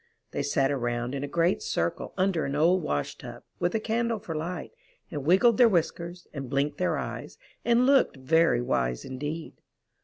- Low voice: No, medium, 160 Hz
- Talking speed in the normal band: Yes, average, 180 wpm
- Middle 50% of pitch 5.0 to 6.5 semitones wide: Yes, average, 5.3 semitones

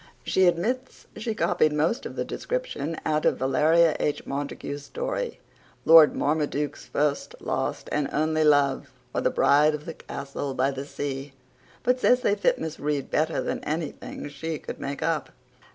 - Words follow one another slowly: No, average, 165 wpm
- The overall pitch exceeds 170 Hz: No, medium, 150 Hz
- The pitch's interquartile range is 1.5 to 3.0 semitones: Yes, narrow, 2.6 semitones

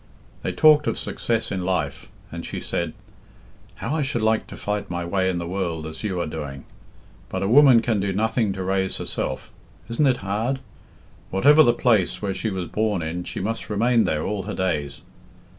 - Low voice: Yes, low, 100 Hz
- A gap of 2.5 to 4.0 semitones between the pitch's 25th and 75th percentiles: No, average, 4.4 semitones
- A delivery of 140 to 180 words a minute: No, average, 195 wpm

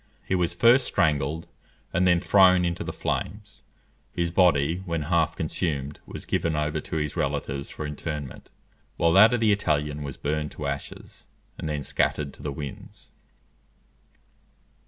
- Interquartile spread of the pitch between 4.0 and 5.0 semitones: No, average, 3.2 semitones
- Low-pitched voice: Yes, very low, 80 Hz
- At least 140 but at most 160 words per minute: Yes, average, 155 wpm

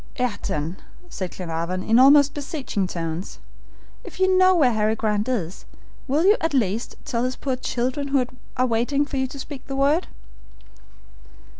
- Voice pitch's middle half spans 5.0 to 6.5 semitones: Yes, wide, 5.4 semitones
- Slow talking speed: No, average, 160 wpm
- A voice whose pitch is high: Yes, very high, 255 Hz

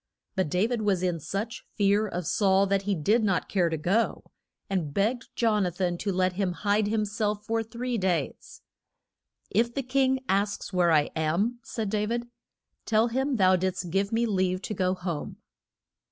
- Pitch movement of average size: Yes, average, 3.5 semitones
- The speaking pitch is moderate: No, high, 200 Hz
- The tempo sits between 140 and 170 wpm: No, average, 190 wpm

